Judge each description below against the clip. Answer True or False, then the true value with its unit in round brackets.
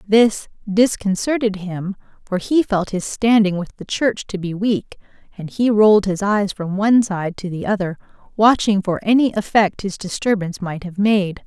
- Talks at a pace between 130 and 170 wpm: False (180 wpm)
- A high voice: True (200 Hz)